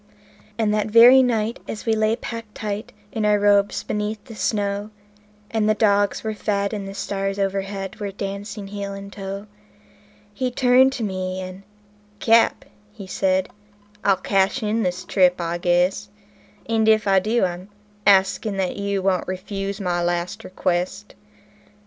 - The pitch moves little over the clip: Yes, narrow, 2.0 semitones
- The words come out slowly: No, average, 155 wpm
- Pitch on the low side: No, high, 200 Hz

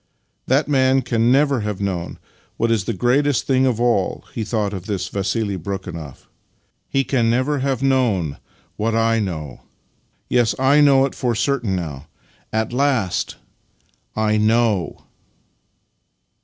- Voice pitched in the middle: No, low, 115 Hz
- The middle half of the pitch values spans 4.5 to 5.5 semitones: Yes, average, 4.9 semitones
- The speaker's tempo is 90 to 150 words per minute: Yes, average, 145 wpm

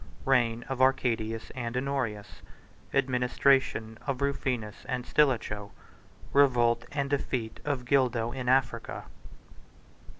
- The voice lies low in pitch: Yes, low, 125 Hz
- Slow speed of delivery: Yes, slow, 90 wpm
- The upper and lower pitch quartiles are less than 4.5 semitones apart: Yes, average, 2.7 semitones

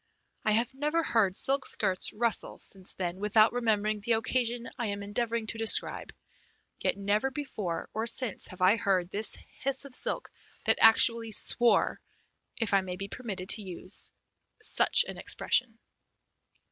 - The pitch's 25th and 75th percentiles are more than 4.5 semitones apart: No, average, 3.2 semitones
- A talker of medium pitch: No, high, 220 Hz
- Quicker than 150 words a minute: Yes, average, 160 wpm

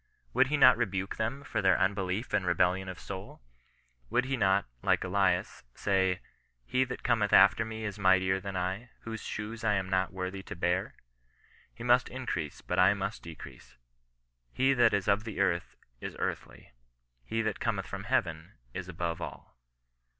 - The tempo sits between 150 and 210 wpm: Yes, average, 180 wpm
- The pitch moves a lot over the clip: No, average, 3.2 semitones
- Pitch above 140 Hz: No, very low, 95 Hz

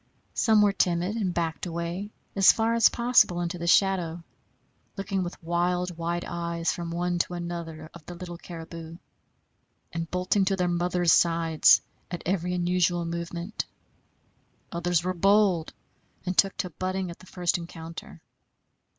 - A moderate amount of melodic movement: No, narrow, 1.5 semitones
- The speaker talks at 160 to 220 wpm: No, average, 150 wpm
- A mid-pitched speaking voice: Yes, medium, 175 Hz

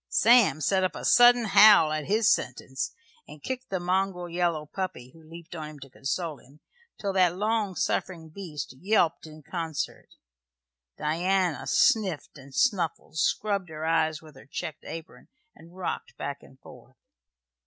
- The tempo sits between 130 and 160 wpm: Yes, average, 155 wpm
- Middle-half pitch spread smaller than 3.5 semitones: No, average, 3.9 semitones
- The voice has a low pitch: No, medium, 170 Hz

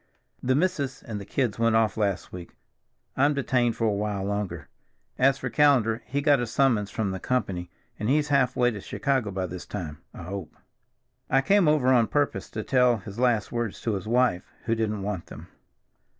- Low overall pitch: Yes, low, 115 Hz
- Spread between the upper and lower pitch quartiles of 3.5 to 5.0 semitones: Yes, average, 4.7 semitones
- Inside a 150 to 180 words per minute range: No, average, 195 wpm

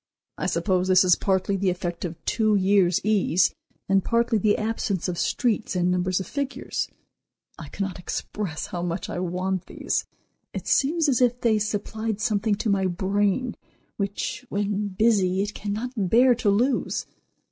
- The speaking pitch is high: Yes, high, 200 Hz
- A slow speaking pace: No, average, 160 wpm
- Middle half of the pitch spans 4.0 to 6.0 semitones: No, average, 3.0 semitones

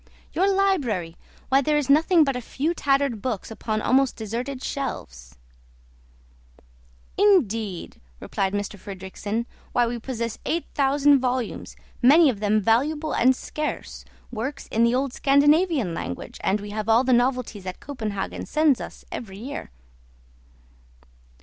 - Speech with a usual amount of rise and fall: Yes, average, 4.8 semitones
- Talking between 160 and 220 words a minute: No, slow, 135 wpm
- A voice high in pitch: Yes, very high, 250 Hz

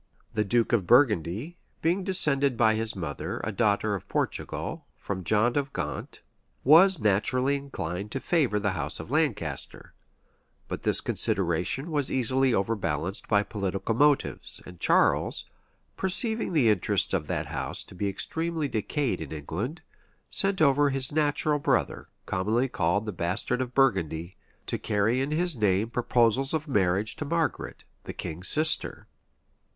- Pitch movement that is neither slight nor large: No, wide, 6.7 semitones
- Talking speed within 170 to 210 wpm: No, average, 145 wpm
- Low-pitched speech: Yes, low, 115 Hz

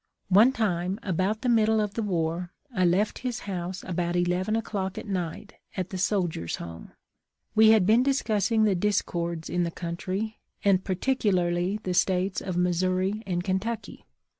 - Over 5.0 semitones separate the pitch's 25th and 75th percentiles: No, average, 3.3 semitones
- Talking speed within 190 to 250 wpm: No, average, 160 wpm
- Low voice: No, high, 190 Hz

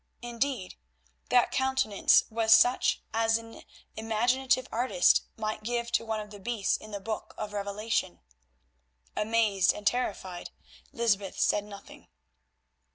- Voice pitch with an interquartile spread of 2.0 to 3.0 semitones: Yes, narrow, 2.4 semitones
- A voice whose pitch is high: Yes, high, 220 Hz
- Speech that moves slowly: Yes, slow, 125 wpm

